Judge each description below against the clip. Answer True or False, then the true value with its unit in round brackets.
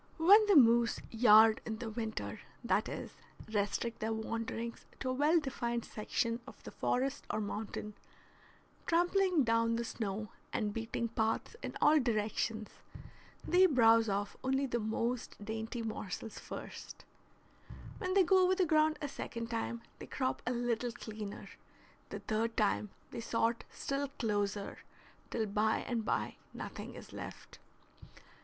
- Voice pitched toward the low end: False (230 Hz)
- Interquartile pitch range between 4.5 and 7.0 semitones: False (3.2 semitones)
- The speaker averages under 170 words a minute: True (145 wpm)